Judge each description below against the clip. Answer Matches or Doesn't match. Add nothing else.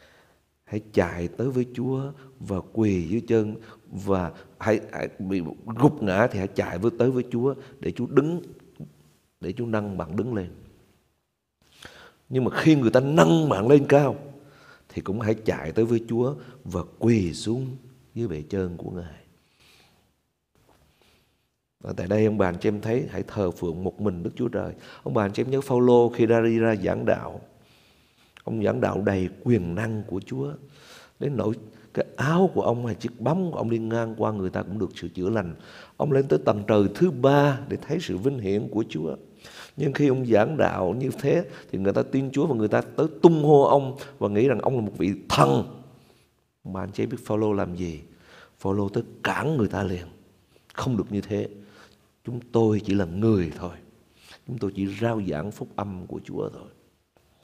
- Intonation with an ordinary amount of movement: Matches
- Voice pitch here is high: Doesn't match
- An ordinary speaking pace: Matches